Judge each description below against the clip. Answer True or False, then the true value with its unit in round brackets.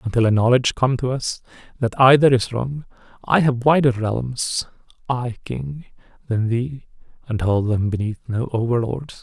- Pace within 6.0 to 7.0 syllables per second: False (4.6 syllables/s)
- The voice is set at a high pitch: False (120 Hz)